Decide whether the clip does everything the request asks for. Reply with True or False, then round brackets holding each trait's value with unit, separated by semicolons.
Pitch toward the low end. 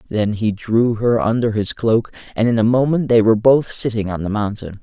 True (110 Hz)